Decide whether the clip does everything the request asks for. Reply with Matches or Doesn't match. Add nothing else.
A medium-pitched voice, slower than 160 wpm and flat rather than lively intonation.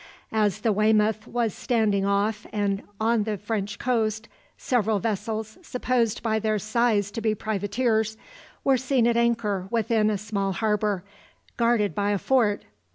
Doesn't match